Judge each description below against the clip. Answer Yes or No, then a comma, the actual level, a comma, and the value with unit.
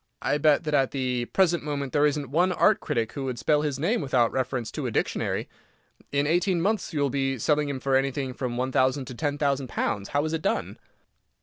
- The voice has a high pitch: No, medium, 140 Hz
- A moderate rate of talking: No, fast, 225 wpm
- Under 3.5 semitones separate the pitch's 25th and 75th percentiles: Yes, narrow, 2.6 semitones